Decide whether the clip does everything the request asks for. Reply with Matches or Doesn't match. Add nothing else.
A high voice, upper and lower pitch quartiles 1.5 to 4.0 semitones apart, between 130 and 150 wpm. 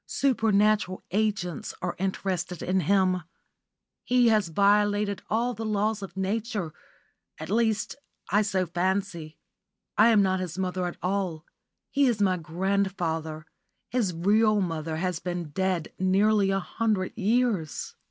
Matches